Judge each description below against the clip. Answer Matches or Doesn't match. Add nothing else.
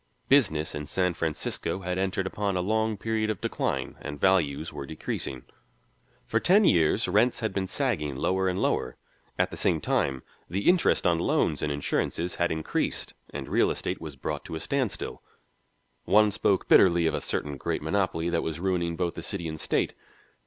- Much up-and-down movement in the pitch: Doesn't match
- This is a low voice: Matches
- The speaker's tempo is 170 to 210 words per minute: Matches